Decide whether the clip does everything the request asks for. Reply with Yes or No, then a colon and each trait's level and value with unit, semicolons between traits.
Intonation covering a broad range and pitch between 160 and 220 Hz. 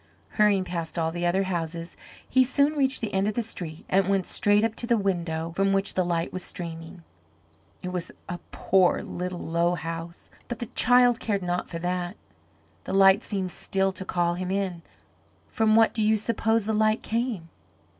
No: average, 3.8 semitones; high, 190 Hz